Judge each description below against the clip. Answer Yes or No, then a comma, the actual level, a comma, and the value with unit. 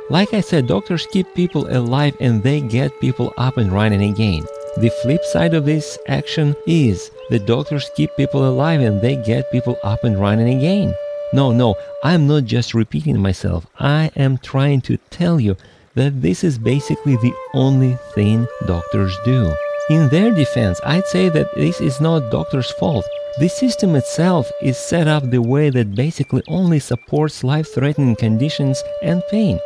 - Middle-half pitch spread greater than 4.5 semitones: Yes, average, 5.1 semitones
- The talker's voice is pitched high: No, medium, 140 Hz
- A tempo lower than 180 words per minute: Yes, average, 170 wpm